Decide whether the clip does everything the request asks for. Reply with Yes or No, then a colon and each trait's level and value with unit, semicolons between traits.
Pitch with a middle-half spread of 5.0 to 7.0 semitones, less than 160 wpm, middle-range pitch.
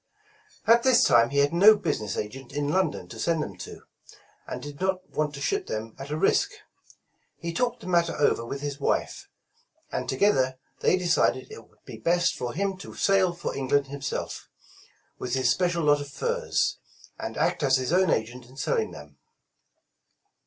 No: wide, 5.4 semitones; average, 185 wpm; medium, 145 Hz